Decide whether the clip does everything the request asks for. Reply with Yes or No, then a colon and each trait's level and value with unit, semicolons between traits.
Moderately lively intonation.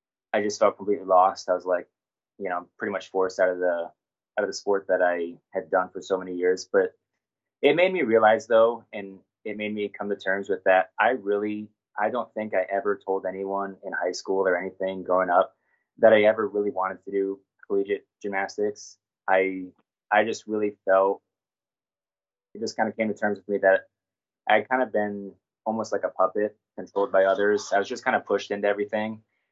No: narrow, 1.9 semitones